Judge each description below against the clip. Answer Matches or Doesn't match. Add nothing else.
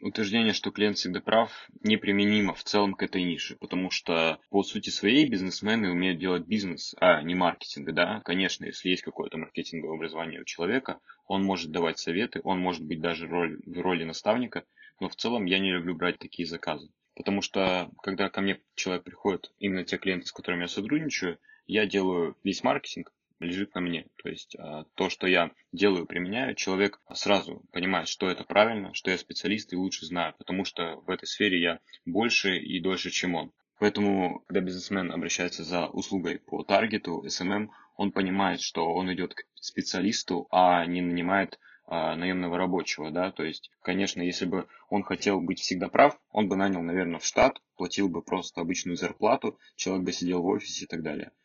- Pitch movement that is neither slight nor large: Doesn't match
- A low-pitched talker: Matches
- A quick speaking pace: Matches